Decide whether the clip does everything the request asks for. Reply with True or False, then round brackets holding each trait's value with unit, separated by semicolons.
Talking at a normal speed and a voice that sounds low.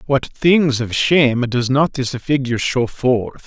True (175 wpm; 130 Hz)